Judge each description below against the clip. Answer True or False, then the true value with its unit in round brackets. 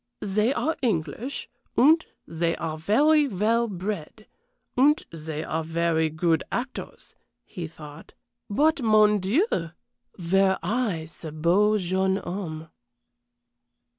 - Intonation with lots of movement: True (5.9 semitones)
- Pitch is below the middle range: False (190 Hz)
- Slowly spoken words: True (110 wpm)